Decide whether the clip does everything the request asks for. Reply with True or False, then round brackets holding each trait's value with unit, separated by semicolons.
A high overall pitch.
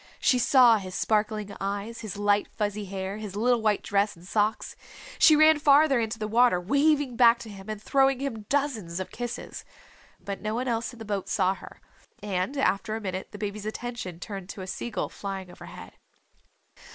True (215 Hz)